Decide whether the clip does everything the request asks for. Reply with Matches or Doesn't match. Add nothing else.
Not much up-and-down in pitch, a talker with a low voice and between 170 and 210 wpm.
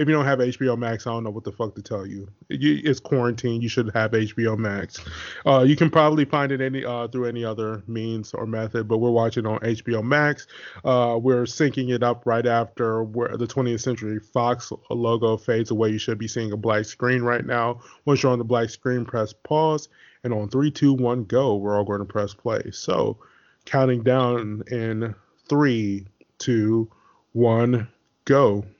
Matches